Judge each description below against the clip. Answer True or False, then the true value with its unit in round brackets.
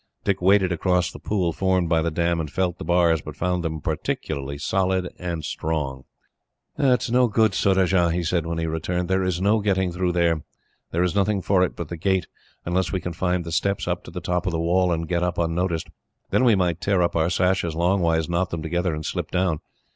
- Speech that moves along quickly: True (225 wpm)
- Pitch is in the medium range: False (90 Hz)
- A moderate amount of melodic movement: False (2.2 semitones)